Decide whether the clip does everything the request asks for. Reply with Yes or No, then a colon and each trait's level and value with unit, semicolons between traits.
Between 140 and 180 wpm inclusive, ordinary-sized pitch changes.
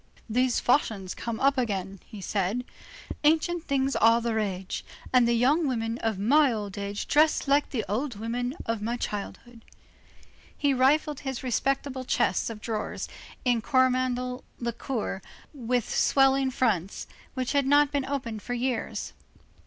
Yes: average, 145 wpm; average, 3.5 semitones